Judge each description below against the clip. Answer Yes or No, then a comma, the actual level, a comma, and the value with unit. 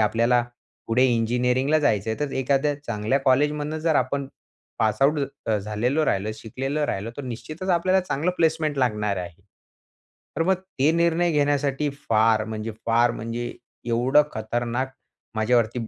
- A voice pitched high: No, low, 130 Hz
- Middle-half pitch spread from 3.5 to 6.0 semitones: Yes, average, 4.8 semitones